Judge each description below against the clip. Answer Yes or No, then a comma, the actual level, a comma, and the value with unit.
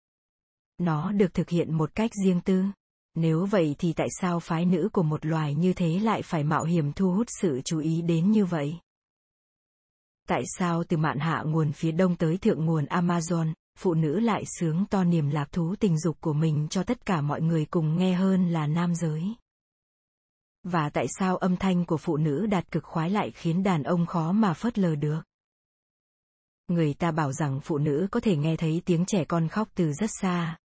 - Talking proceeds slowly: No, average, 205 wpm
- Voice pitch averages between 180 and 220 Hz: No, medium, 170 Hz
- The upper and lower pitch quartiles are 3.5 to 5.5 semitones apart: No, average, 2.8 semitones